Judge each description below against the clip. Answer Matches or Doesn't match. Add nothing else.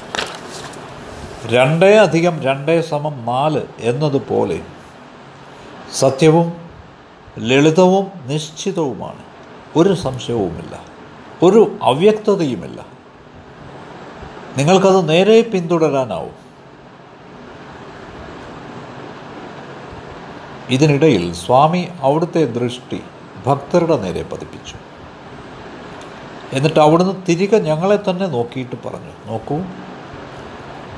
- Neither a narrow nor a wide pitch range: Doesn't match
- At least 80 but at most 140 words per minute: Doesn't match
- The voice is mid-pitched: Matches